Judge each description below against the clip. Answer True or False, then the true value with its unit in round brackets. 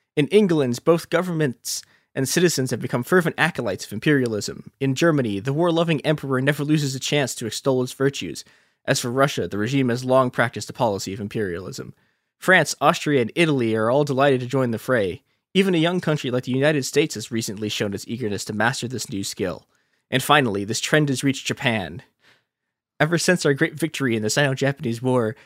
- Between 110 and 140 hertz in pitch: True (135 Hz)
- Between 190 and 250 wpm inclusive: True (200 wpm)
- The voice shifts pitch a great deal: False (4.3 semitones)